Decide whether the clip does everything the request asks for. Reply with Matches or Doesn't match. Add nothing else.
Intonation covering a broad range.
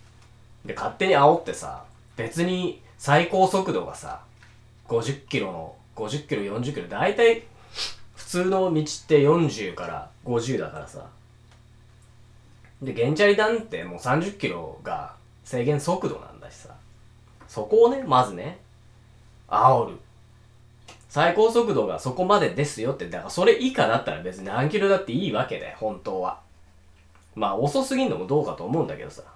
Matches